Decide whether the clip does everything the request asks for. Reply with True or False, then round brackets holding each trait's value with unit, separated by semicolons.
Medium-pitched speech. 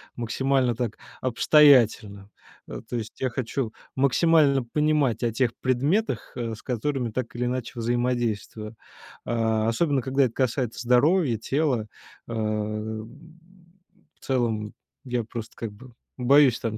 False (120 Hz)